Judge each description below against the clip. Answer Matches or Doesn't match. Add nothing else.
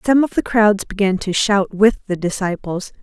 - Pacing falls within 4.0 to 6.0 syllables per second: Matches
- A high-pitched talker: Matches